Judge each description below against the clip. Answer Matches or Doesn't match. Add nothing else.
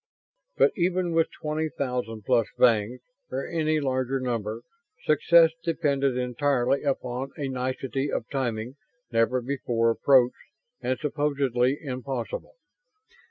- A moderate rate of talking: Doesn't match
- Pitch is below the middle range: Matches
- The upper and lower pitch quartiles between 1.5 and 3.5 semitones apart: Matches